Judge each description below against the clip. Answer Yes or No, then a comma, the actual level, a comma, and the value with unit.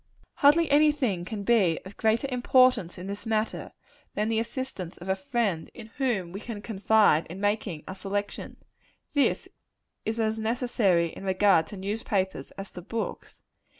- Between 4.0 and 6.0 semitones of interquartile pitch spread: No, average, 3.6 semitones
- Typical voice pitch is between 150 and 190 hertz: No, high, 210 Hz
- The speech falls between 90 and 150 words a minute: No, average, 160 wpm